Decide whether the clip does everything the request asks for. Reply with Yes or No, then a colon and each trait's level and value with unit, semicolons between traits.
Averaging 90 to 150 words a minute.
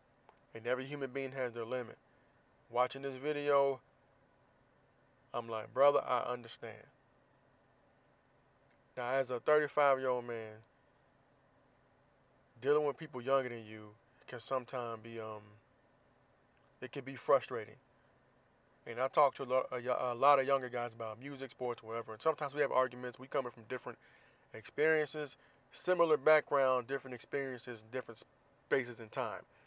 Yes: average, 140 wpm